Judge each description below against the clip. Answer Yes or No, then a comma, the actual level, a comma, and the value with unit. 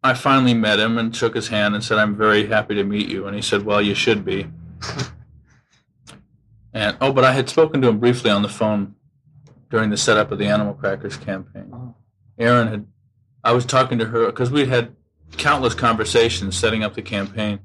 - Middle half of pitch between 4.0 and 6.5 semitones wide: No, average, 3.0 semitones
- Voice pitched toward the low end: Yes, low, 110 Hz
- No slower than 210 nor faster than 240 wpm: No, average, 200 wpm